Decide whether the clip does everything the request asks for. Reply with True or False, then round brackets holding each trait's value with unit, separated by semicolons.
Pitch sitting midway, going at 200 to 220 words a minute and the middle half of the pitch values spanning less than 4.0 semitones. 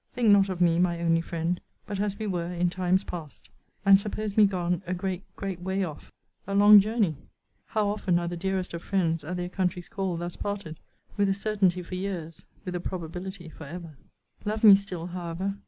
True (180 Hz; 205 wpm; 2.5 semitones)